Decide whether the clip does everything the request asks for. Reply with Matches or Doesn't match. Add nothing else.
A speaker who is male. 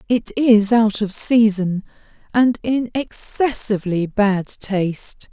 Doesn't match